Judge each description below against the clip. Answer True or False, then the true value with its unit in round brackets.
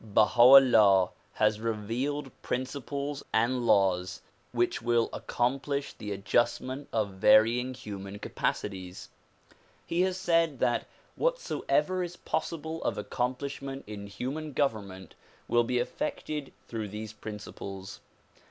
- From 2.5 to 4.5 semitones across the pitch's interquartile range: False (5.1 semitones)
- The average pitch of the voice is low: True (120 Hz)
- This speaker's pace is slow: True (115 wpm)